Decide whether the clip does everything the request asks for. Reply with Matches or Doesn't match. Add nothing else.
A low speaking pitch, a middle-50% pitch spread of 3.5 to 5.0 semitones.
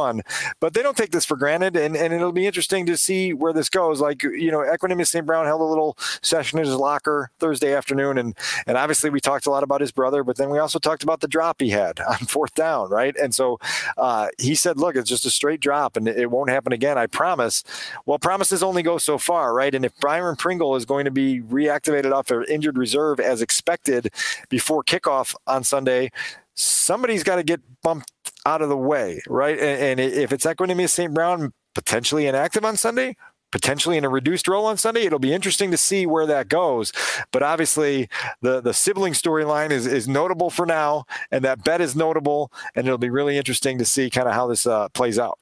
Doesn't match